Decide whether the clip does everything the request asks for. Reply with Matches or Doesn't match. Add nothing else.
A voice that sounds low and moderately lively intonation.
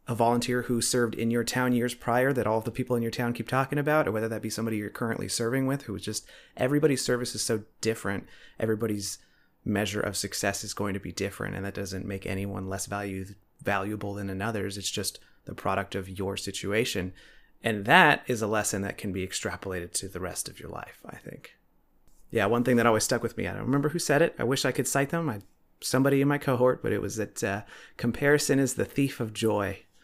Matches